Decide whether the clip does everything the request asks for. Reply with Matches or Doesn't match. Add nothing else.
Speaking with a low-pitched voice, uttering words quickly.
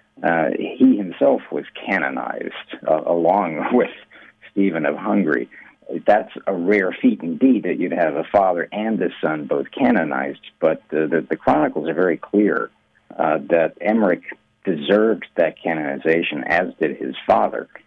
Doesn't match